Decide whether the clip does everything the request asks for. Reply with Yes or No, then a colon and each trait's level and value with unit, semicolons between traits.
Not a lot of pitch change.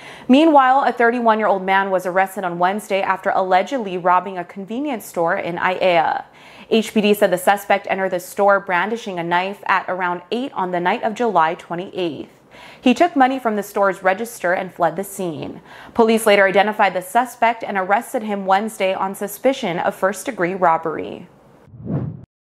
No: average, 3.4 semitones